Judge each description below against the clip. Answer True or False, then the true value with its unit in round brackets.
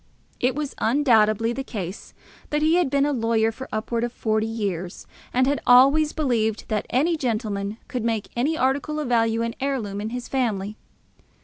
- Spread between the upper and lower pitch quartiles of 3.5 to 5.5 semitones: True (3.8 semitones)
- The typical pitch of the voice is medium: False (235 Hz)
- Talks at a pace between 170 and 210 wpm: True (180 wpm)